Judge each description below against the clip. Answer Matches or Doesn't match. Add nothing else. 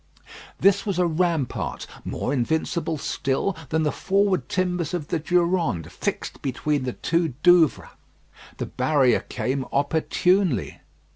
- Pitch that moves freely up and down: Doesn't match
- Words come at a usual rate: Doesn't match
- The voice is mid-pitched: Matches